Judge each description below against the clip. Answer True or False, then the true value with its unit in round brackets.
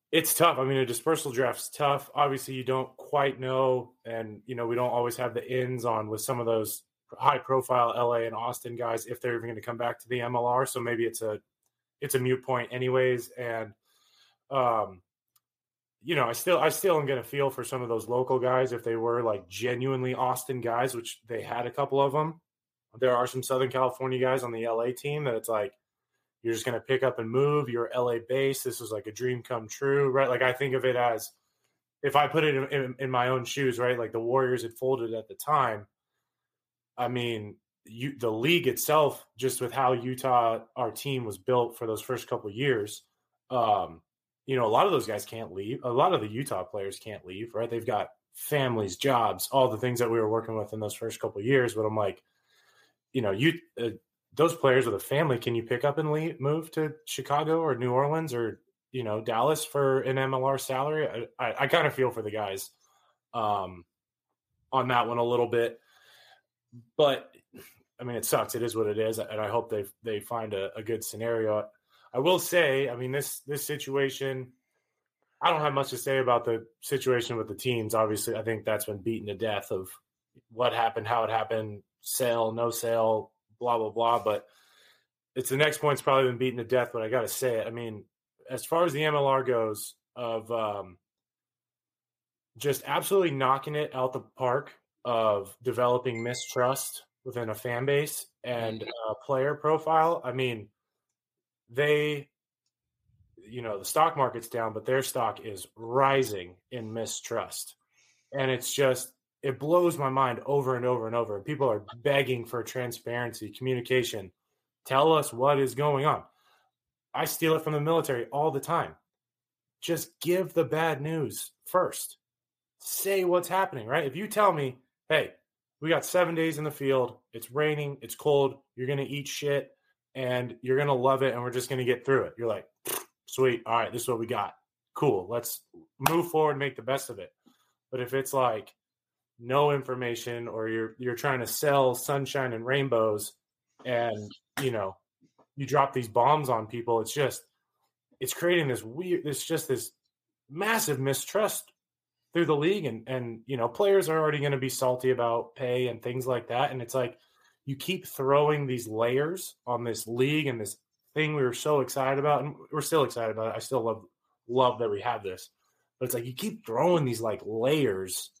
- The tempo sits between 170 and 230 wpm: True (200 wpm)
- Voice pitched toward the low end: True (125 Hz)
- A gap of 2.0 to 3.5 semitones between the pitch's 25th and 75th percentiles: True (3.0 semitones)